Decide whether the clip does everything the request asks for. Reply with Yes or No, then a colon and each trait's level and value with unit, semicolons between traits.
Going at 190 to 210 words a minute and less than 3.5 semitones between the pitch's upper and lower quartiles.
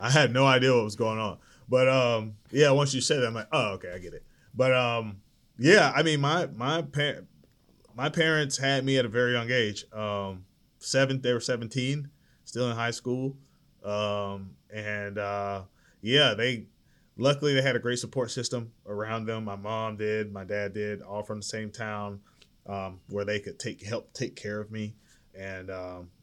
No: average, 195 wpm; average, 3.9 semitones